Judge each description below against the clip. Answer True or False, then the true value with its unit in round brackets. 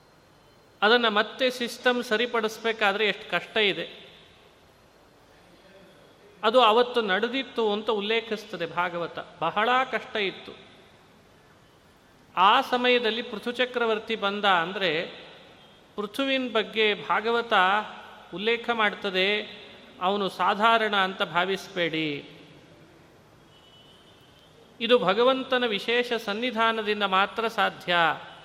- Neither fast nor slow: True (80 wpm)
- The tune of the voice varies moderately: True (3.7 semitones)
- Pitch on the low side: False (215 Hz)